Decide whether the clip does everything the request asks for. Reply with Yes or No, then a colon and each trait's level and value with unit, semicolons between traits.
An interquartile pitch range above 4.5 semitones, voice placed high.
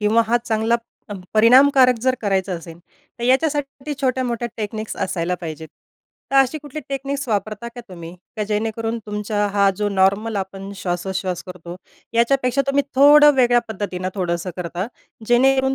Yes: average, 5.3 semitones; high, 220 Hz